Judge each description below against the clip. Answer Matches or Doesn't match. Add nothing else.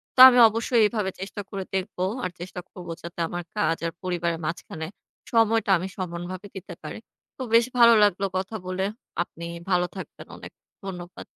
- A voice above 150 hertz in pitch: Matches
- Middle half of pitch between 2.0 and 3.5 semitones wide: Matches